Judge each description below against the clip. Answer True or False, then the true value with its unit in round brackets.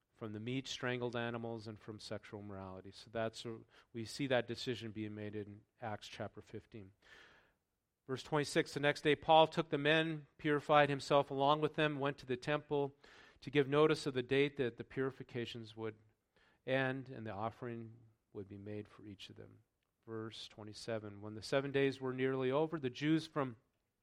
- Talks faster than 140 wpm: True (180 wpm)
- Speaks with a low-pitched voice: True (120 Hz)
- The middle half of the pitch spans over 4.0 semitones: True (4.4 semitones)